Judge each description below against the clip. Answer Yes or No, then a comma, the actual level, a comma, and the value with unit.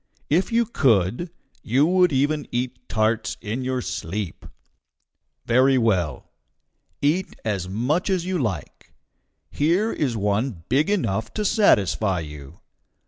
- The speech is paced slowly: Yes, slow, 125 wpm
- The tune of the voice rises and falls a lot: Yes, wide, 7.9 semitones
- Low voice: Yes, low, 125 Hz